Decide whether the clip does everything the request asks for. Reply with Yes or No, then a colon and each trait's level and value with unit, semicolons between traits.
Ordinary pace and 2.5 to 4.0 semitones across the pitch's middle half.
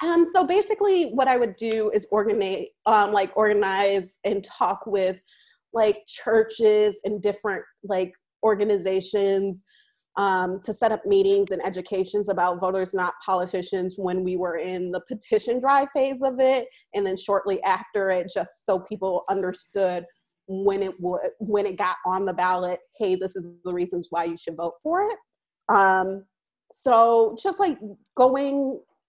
Yes: average, 155 wpm; average, 3.6 semitones